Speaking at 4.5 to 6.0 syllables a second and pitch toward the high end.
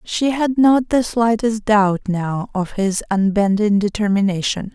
No: 4.0 syllables/s; high, 210 Hz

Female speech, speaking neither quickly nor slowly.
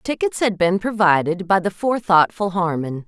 Yes: female; average, 155 wpm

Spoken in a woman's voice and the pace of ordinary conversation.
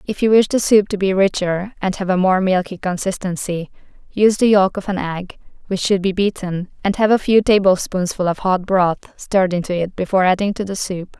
No: female; fast, 215 wpm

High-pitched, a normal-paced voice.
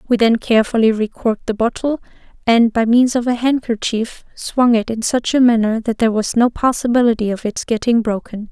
Yes: high, 230 Hz; average, 190 wpm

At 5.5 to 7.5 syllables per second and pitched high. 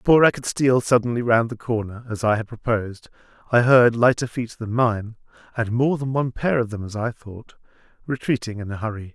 No: 5.7 syllables/s; low, 115 Hz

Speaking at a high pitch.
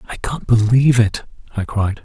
No: low, 110 Hz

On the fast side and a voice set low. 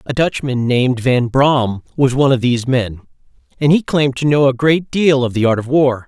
Yes: fast, 245 wpm; low, 130 Hz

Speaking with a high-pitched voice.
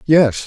No: medium, 140 Hz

